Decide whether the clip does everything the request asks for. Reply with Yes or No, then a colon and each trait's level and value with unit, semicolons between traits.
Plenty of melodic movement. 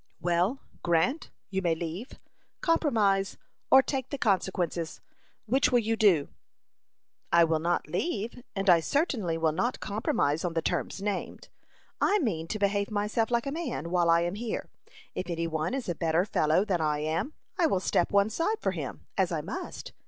Yes: wide, 5.7 semitones